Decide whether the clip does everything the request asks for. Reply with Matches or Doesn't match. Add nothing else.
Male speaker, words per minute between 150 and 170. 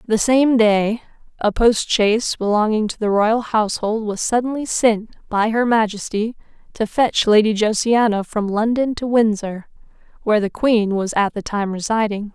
Doesn't match